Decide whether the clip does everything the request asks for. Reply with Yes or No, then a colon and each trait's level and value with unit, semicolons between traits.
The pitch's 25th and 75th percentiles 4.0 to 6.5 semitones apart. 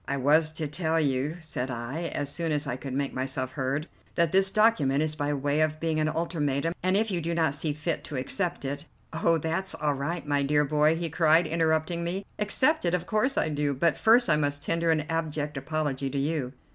No: average, 2.8 semitones